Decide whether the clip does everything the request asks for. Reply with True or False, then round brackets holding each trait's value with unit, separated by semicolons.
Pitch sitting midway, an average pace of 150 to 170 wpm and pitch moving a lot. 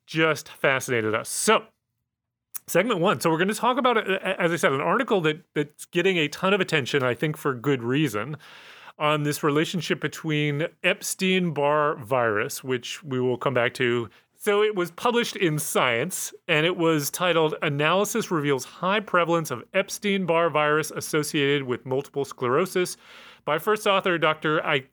False (160 Hz; 160 wpm; 4.5 semitones)